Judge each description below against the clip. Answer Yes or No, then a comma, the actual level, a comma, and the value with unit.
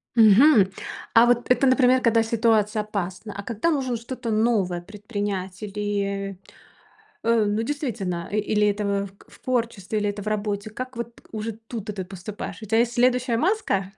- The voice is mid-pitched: No, high, 215 Hz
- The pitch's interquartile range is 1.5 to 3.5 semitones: Yes, average, 2.8 semitones